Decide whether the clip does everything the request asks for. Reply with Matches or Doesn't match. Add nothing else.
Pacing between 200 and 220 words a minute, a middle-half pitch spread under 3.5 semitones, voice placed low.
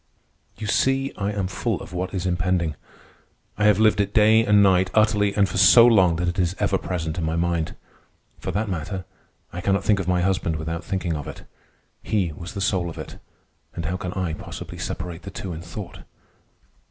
Matches